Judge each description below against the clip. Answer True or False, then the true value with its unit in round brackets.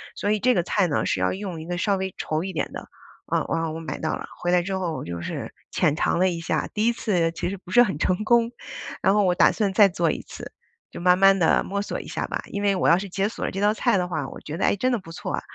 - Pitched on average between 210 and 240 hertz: False (185 Hz)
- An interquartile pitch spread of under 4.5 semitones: True (3.3 semitones)